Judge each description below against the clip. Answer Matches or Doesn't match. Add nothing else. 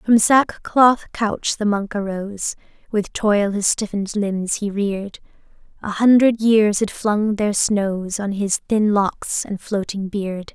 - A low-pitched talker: Doesn't match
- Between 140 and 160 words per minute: Matches